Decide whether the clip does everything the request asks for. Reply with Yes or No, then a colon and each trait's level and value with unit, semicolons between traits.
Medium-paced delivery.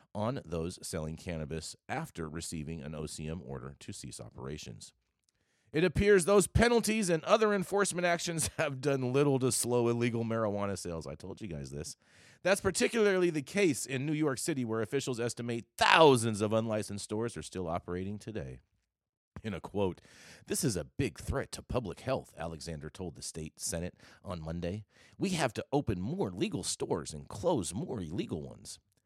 Yes: average, 170 wpm